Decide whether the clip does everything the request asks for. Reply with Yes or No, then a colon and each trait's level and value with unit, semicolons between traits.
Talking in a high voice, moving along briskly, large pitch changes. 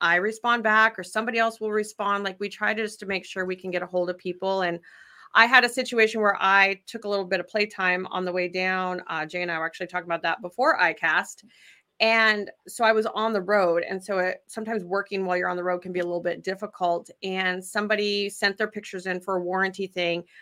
No: high, 195 Hz; fast, 250 wpm; average, 3.0 semitones